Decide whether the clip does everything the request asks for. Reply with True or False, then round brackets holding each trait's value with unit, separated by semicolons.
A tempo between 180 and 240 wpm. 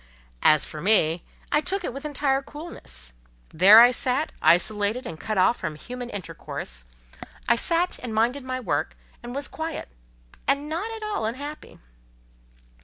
False (155 wpm)